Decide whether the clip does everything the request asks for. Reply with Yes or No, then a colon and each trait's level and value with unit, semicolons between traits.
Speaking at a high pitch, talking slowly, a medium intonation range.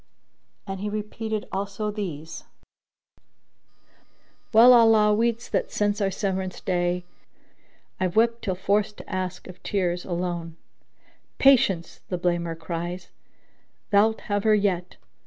Yes: high, 195 Hz; slow, 130 wpm; average, 3.0 semitones